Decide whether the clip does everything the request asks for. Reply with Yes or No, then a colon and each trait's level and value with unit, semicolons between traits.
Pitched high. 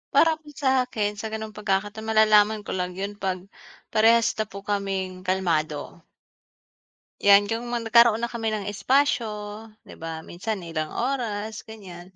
Yes: high, 210 Hz